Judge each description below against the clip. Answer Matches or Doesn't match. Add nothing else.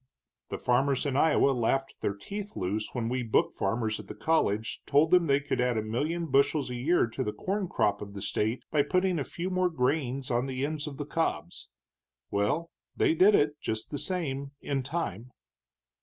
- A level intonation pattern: Doesn't match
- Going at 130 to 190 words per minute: Doesn't match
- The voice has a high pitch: Doesn't match